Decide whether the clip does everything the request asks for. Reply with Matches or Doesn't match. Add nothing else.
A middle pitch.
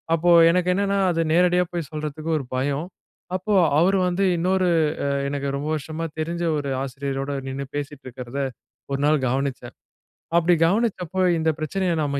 Matches